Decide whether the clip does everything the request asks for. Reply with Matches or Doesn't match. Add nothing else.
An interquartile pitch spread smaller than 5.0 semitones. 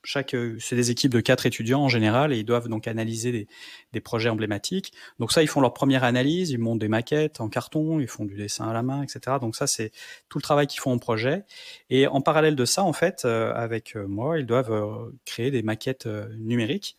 Matches